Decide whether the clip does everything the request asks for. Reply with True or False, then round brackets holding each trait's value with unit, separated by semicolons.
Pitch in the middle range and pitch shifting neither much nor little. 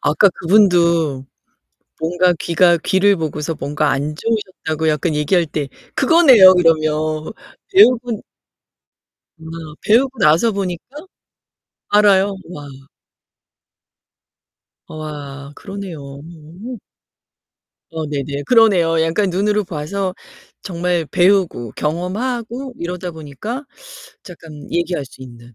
True (170 Hz; 4.7 semitones)